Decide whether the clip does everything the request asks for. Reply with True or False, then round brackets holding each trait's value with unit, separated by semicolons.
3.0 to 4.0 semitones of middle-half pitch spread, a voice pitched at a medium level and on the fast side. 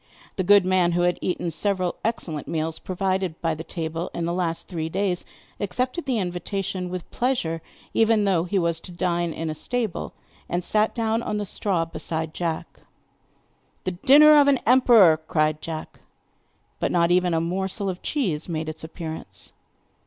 False (3.6 semitones; 180 Hz; 170 wpm)